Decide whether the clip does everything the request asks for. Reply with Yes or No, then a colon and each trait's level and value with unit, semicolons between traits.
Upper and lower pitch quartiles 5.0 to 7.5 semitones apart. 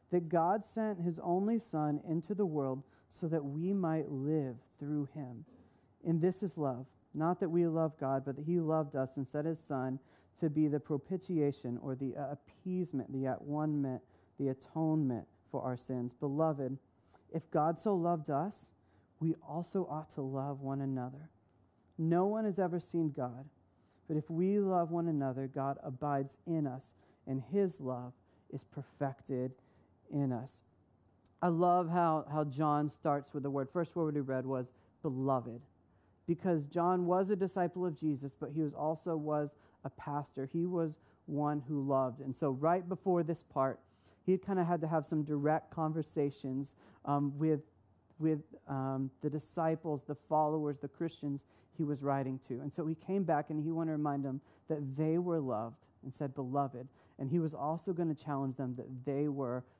No: average, 3.6 semitones